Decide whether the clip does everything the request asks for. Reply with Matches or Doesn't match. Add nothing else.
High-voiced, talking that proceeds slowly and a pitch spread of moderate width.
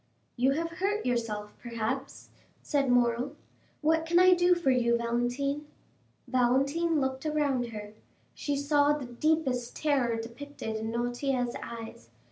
Matches